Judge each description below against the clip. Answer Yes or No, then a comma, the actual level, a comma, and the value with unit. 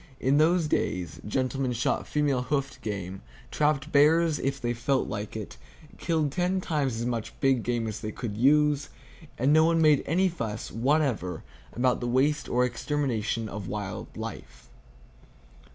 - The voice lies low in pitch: Yes, low, 130 Hz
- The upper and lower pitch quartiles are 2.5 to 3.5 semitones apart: No, average, 4.8 semitones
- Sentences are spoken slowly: No, average, 155 wpm